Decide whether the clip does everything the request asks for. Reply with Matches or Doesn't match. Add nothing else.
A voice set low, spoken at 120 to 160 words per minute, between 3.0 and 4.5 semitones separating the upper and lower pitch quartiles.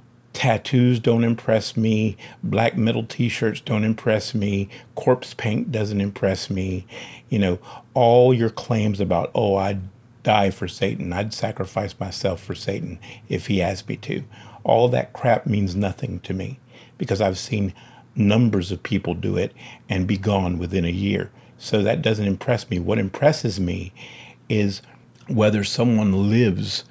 Matches